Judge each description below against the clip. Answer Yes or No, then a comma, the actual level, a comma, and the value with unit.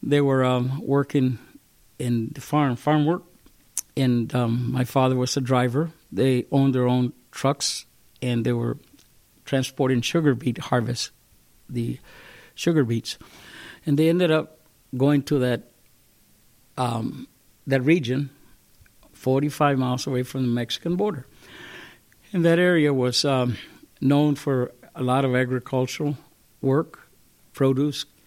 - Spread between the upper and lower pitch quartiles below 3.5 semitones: Yes, average, 2.7 semitones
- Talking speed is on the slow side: Yes, slow, 130 wpm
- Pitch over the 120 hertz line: Yes, low, 135 Hz